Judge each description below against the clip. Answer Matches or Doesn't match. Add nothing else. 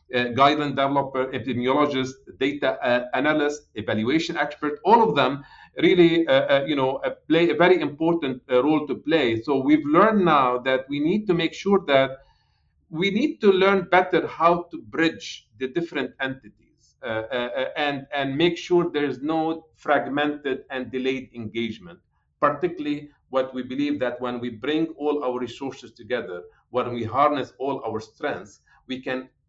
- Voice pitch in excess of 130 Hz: Matches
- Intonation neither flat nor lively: Matches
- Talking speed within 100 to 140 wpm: Doesn't match